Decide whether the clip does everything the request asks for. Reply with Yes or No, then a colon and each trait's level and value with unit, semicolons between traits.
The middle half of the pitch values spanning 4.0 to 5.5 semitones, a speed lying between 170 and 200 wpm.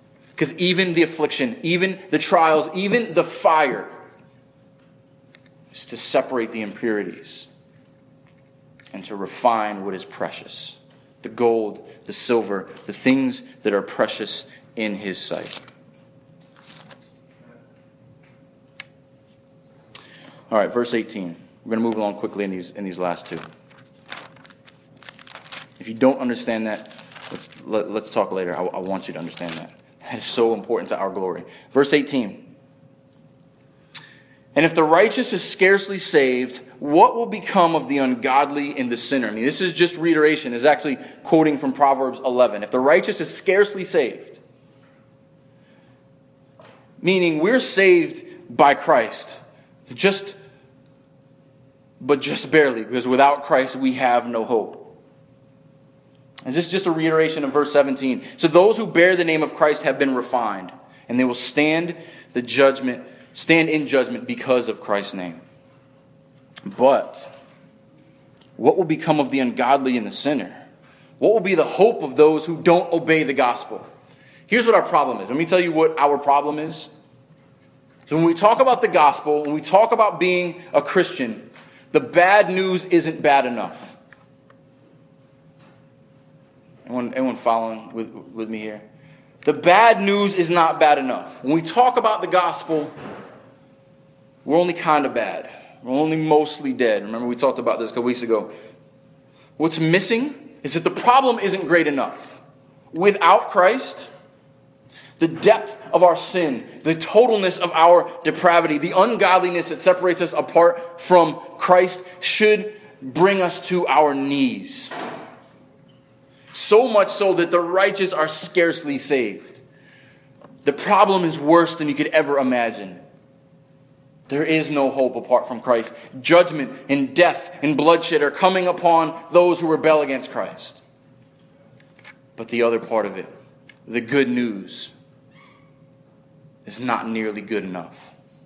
No: average, 5.1 semitones; average, 145 wpm